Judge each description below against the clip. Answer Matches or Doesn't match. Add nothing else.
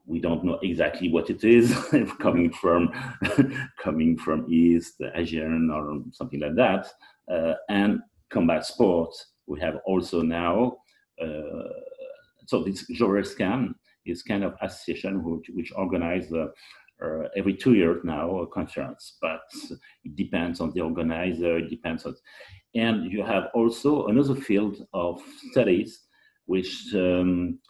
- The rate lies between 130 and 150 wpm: Matches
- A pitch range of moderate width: Doesn't match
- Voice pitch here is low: Matches